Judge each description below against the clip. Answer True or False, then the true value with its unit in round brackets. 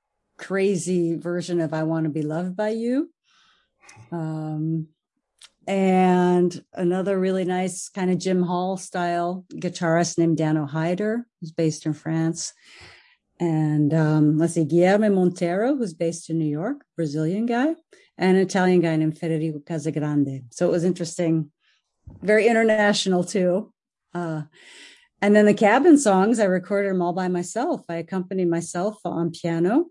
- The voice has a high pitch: False (180 Hz)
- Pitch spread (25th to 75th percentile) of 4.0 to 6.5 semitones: False (3.4 semitones)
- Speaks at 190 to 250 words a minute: False (145 wpm)